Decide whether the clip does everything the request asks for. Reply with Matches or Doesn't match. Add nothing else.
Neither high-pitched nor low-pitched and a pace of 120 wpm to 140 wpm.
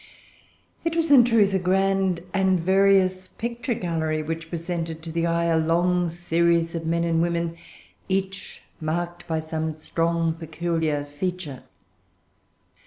Matches